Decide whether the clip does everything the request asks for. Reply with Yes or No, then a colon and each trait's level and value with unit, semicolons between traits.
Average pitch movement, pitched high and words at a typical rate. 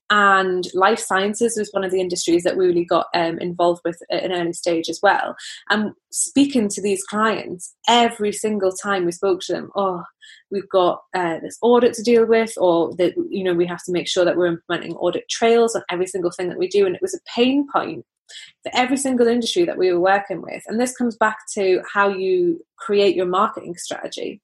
No: average, 4.6 semitones; high, 195 Hz; fast, 220 wpm